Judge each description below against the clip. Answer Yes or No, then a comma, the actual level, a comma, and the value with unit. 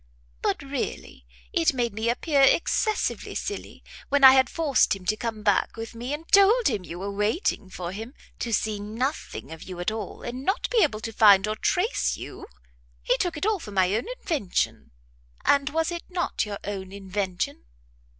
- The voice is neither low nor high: No, high, 225 Hz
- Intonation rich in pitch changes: Yes, wide, 6.7 semitones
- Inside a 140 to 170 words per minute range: No, average, 190 wpm